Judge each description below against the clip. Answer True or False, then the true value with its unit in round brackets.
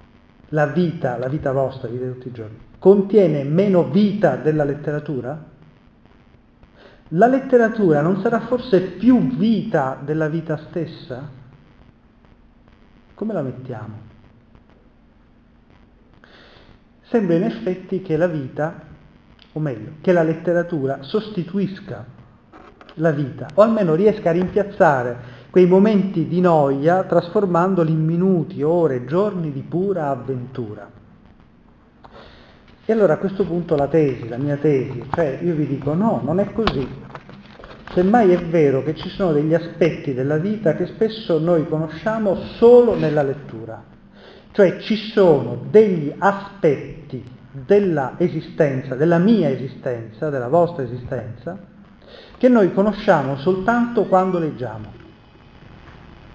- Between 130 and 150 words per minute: False (120 wpm)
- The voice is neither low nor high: True (165 Hz)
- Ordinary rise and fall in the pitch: False (5.9 semitones)